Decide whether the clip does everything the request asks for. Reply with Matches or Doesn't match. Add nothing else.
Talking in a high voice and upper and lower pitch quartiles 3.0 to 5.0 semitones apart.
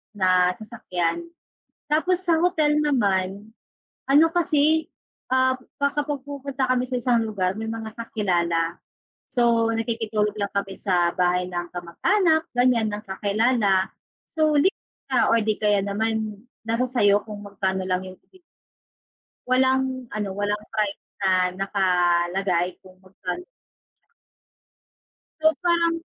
Doesn't match